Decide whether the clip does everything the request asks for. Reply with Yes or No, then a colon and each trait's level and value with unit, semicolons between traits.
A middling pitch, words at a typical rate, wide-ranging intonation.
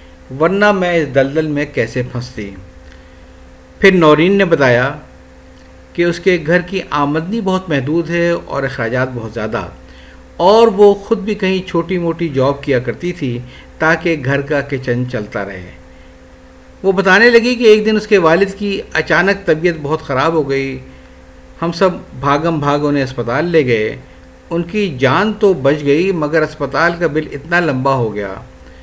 Yes: medium, 145 Hz; average, 165 wpm; wide, 7.4 semitones